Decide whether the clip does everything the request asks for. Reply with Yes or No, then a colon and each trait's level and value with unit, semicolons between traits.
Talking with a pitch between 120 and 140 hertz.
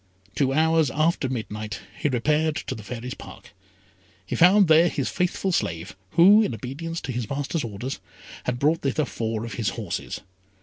Yes: low, 135 Hz